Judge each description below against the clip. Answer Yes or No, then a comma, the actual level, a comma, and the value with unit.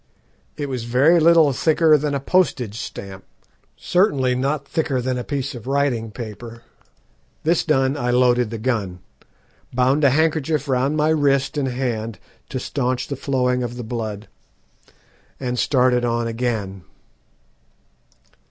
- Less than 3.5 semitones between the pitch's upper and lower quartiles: Yes, average, 3.1 semitones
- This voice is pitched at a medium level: No, low, 130 Hz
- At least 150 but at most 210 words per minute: No, average, 140 wpm